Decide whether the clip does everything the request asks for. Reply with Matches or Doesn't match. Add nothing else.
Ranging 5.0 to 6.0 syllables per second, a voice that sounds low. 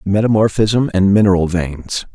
Doesn't match